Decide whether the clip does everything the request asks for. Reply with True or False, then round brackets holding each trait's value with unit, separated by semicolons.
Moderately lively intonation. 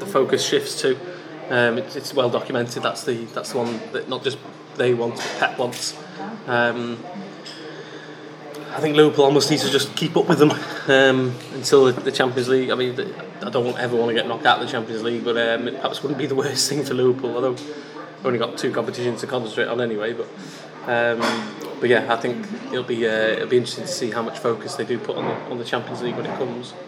True (3.6 semitones)